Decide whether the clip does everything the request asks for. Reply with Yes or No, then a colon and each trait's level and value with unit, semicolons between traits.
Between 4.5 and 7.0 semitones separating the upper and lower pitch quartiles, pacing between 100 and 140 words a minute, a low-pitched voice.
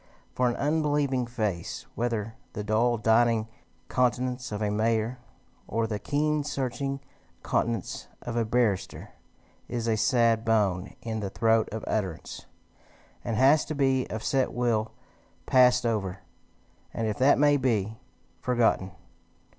No: average, 2.8 semitones; slow, 135 wpm; low, 115 Hz